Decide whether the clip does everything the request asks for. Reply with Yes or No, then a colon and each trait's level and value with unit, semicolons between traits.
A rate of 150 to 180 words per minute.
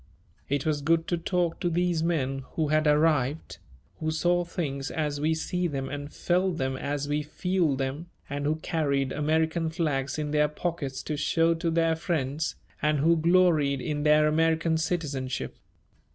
Yes: average, 165 wpm